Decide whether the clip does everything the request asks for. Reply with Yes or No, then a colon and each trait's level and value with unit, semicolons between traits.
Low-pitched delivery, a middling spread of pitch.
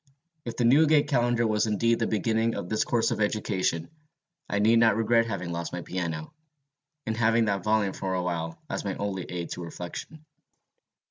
Yes: low, 110 Hz; average, 4.2 semitones